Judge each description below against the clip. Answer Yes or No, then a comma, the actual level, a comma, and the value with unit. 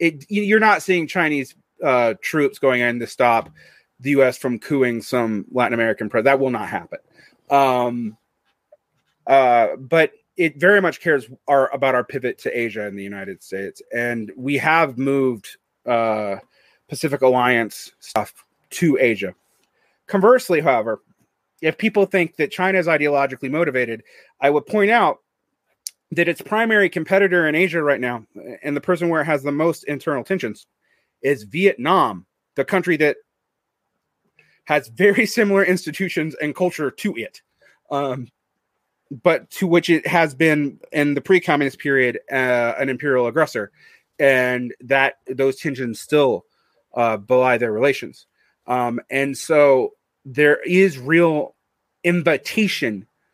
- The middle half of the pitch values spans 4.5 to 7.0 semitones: Yes, wide, 5.4 semitones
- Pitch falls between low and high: Yes, medium, 145 Hz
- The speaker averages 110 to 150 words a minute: Yes, average, 140 wpm